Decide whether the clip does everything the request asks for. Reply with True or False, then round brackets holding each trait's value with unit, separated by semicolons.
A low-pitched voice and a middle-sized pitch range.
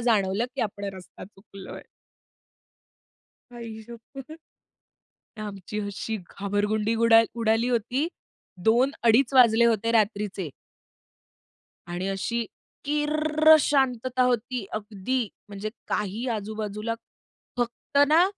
False (225 Hz; 3.3 semitones)